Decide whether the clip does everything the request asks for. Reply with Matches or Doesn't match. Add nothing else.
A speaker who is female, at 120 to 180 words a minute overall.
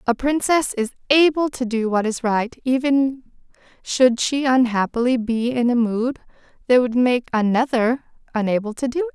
Matches